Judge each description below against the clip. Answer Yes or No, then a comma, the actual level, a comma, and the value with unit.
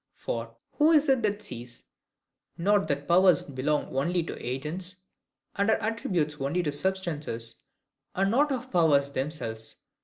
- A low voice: No, medium, 165 Hz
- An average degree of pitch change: No, wide, 6.3 semitones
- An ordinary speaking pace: Yes, average, 145 wpm